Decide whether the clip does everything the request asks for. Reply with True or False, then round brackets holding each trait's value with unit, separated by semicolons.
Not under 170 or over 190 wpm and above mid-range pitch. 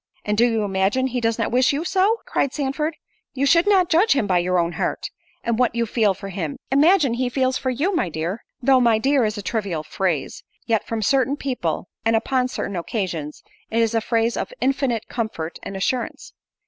False (205 wpm; 230 Hz)